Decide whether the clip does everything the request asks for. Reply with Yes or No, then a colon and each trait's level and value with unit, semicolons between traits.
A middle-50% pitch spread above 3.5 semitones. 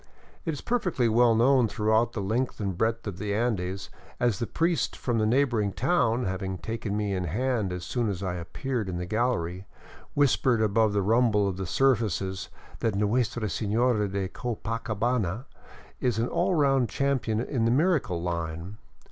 Yes: average, 4.0 semitones